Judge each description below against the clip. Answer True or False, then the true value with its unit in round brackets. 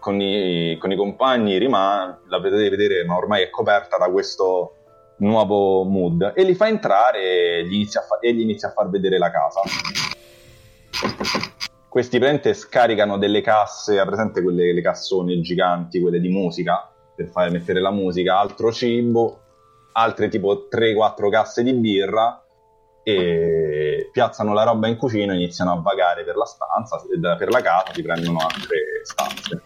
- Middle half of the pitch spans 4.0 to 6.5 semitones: True (4.8 semitones)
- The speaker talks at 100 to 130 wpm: False (160 wpm)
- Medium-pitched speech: False (100 Hz)